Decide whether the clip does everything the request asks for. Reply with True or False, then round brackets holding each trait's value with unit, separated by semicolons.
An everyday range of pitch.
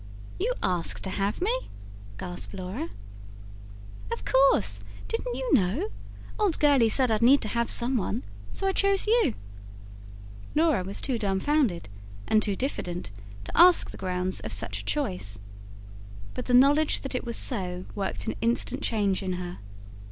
False (7.8 semitones)